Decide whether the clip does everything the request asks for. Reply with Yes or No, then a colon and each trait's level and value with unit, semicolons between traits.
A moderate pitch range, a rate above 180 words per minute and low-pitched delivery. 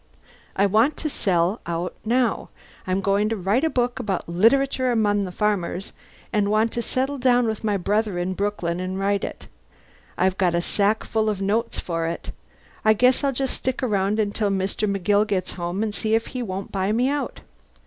No: average, 3.3 semitones; average, 190 wpm; high, 205 Hz